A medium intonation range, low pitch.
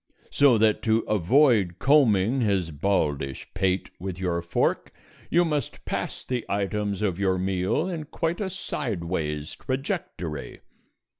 No: wide, 6.8 semitones; low, 100 Hz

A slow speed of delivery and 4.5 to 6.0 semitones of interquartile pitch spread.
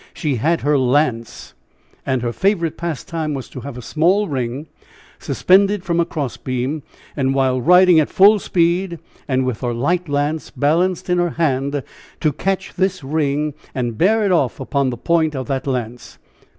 No: average, 165 wpm; average, 4.9 semitones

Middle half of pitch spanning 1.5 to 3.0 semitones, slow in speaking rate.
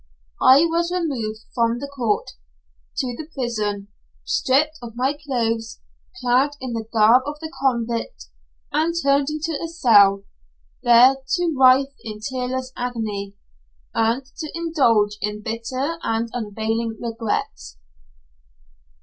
No: average, 3.9 semitones; slow, 125 wpm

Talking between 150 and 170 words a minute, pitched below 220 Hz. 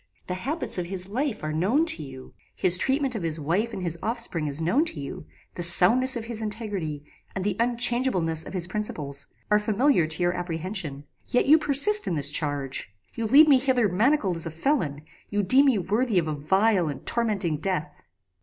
No: average, 200 wpm; high, 190 Hz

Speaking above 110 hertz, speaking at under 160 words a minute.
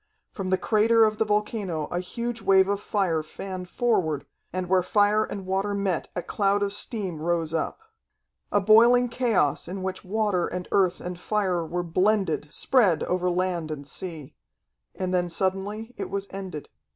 No: high, 190 Hz; average, 170 wpm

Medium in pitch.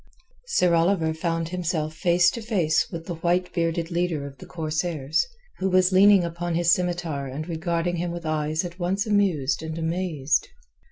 Yes: medium, 170 Hz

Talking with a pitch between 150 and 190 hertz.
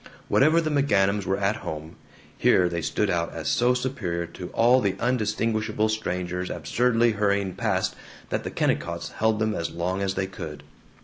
No: low, 100 Hz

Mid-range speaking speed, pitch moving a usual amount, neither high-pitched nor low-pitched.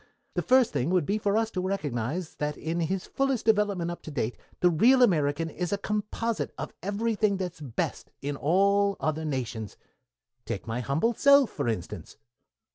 No: average, 180 wpm; wide, 6.0 semitones; medium, 180 Hz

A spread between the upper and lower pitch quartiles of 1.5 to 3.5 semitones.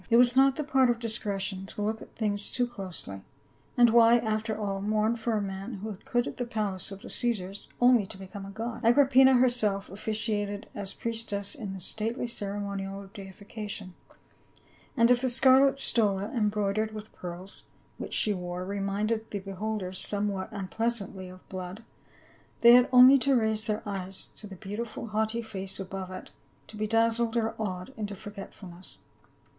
Yes: average, 2.9 semitones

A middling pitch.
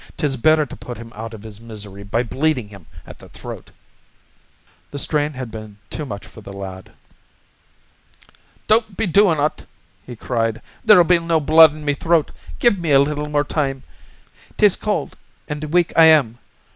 Yes: medium, 145 Hz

